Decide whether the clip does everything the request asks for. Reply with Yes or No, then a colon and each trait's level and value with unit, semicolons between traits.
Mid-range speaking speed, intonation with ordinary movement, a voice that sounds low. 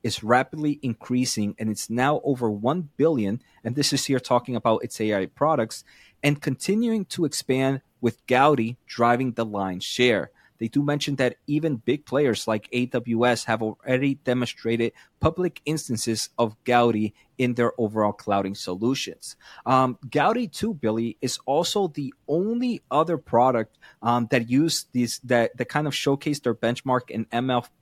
Yes: average, 155 wpm; average, 4.0 semitones; low, 125 Hz